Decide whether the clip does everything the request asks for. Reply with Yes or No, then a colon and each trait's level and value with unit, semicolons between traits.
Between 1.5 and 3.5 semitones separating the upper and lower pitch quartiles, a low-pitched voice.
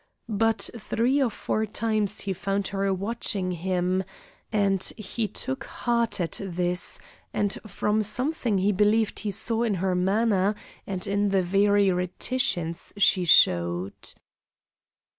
No: average, 2.9 semitones; high, 200 Hz